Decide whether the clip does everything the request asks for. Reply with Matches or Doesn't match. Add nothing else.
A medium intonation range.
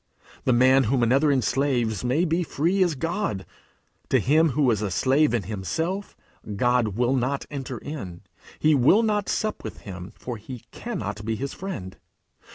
Doesn't match